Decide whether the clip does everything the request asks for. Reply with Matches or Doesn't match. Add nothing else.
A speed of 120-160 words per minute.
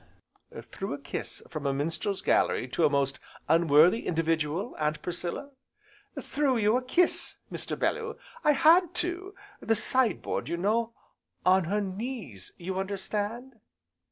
Matches